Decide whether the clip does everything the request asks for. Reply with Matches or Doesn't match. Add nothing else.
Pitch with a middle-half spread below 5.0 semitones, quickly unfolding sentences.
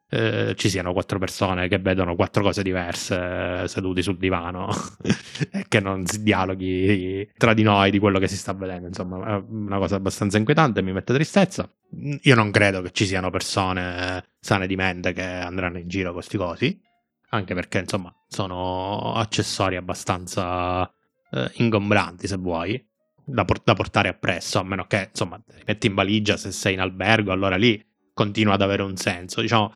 Matches